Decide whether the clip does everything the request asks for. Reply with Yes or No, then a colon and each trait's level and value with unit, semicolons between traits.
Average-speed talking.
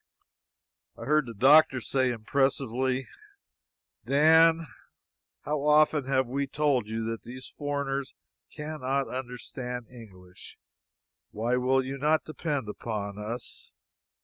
No: slow, 110 wpm